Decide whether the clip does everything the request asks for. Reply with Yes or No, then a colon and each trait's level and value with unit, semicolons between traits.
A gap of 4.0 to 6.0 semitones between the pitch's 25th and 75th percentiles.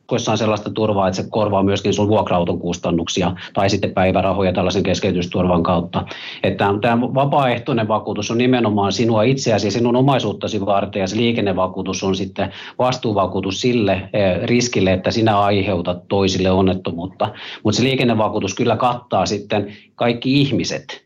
No: average, 3.5 semitones